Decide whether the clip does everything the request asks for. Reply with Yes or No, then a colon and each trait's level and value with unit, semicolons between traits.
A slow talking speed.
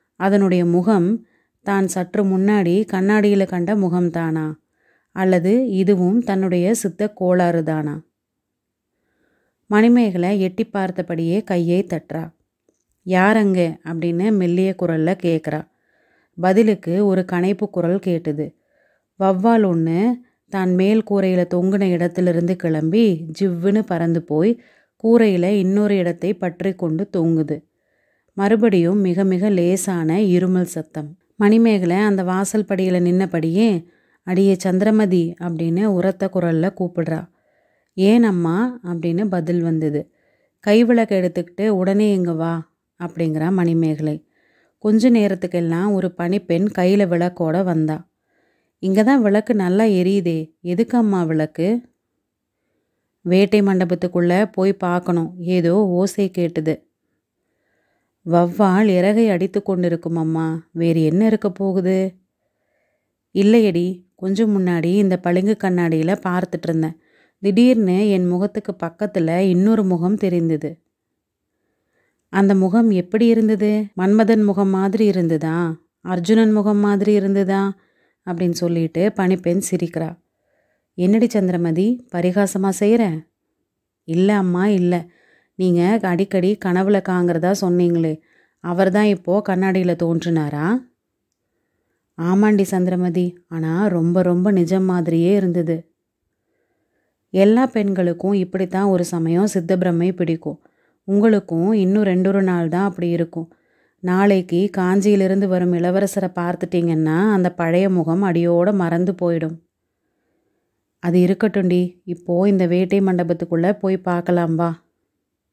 No: average, 105 wpm